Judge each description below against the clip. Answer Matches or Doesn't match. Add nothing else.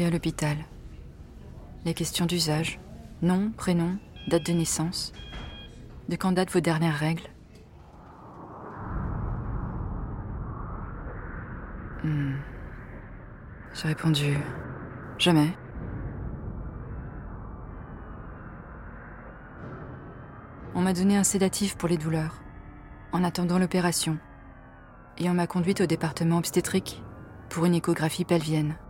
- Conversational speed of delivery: Doesn't match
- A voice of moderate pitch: Matches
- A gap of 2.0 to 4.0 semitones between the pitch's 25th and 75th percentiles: Doesn't match